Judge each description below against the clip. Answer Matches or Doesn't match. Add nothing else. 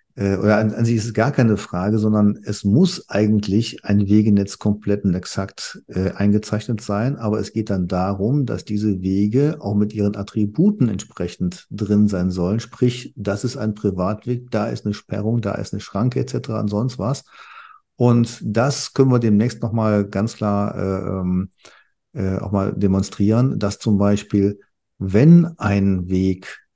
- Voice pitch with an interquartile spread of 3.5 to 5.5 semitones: Doesn't match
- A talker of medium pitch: Doesn't match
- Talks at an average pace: Matches